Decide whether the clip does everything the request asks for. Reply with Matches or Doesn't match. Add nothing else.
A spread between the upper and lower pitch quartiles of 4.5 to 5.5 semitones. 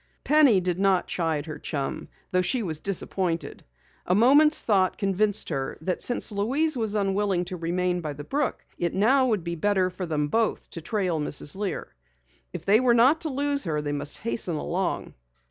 Matches